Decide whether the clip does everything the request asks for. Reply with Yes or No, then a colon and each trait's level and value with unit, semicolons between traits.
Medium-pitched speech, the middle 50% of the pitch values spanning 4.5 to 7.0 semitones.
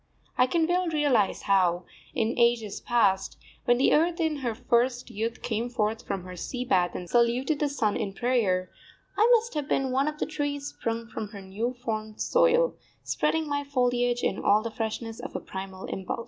No: high, 240 Hz; average, 5.2 semitones